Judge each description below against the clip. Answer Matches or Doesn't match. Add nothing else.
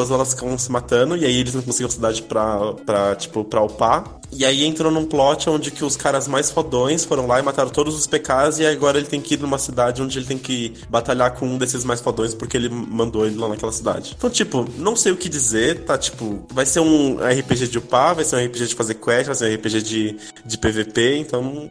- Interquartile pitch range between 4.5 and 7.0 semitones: Doesn't match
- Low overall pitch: Matches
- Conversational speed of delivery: Doesn't match